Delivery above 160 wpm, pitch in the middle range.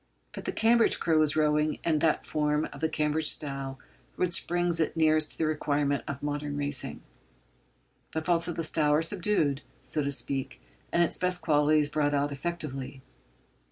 Yes: average, 175 wpm; medium, 150 Hz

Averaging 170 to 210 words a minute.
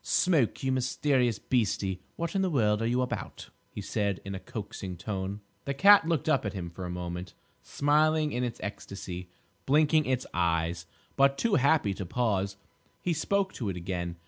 Yes: average, 180 wpm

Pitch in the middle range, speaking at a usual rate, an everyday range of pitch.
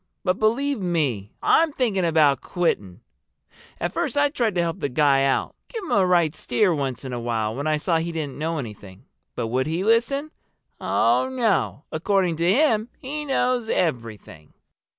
No: medium, 170 Hz; average, 170 wpm; wide, 8.6 semitones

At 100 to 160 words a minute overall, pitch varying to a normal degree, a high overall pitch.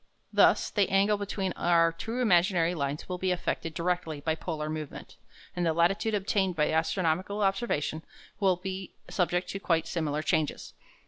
No: average, 155 wpm; average, 3.2 semitones; medium, 175 Hz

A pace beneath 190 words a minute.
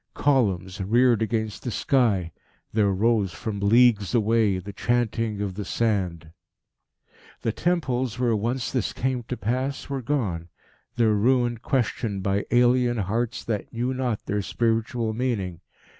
Yes: average, 140 wpm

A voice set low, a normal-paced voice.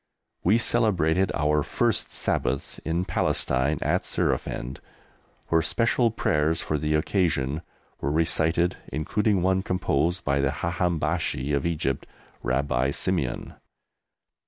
No: very low, 80 Hz; slow, 115 wpm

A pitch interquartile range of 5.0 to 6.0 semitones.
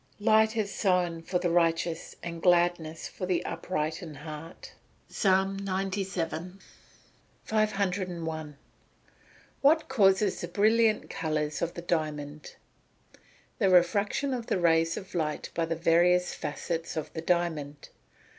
No: average, 3.1 semitones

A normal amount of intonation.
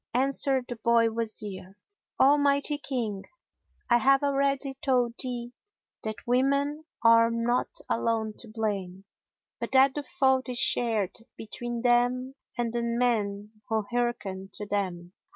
Yes: average, 3.3 semitones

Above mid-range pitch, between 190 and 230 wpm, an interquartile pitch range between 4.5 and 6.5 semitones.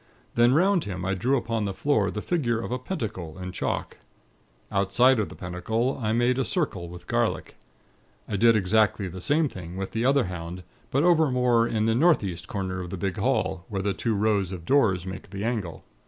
No: low, 105 Hz; fast, 205 wpm; average, 5.1 semitones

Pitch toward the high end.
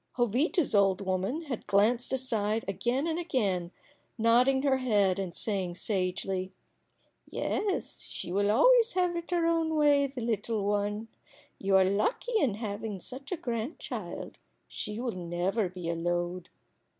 Yes: high, 220 Hz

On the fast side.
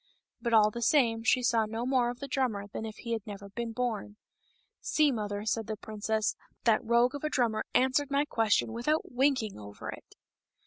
Yes: fast, 210 wpm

